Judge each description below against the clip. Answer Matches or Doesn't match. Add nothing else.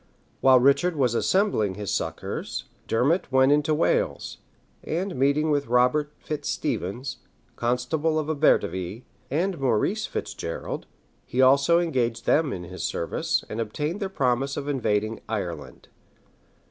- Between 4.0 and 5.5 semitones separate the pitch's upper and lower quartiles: Matches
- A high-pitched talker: Doesn't match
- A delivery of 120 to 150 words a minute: Matches